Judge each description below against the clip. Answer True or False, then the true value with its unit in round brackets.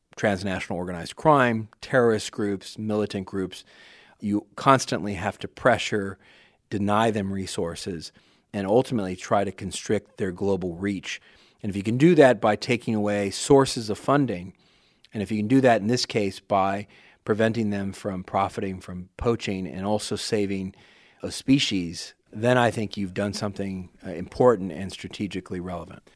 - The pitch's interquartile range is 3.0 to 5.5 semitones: False (2.6 semitones)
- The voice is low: True (100 Hz)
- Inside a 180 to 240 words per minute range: False (150 wpm)